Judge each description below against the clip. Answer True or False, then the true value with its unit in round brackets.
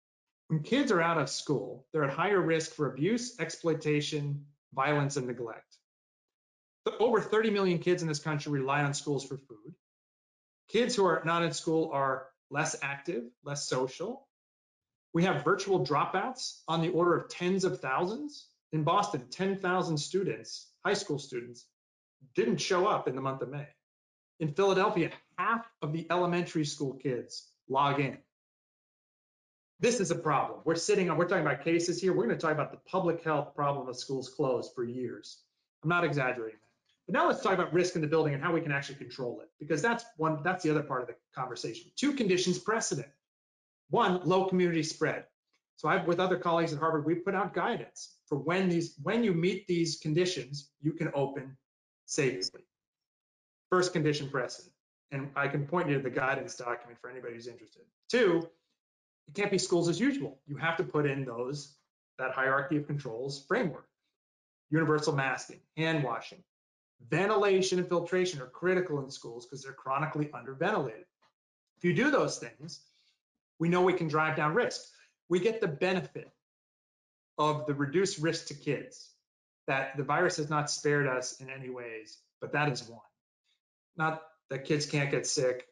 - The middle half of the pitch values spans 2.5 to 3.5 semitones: False (4.4 semitones)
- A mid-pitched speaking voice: True (155 Hz)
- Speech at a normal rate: True (175 wpm)